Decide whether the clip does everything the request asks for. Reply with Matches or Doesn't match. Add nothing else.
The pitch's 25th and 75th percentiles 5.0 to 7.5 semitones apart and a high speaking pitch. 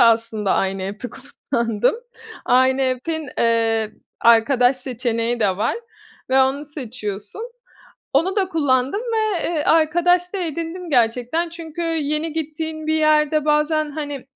Matches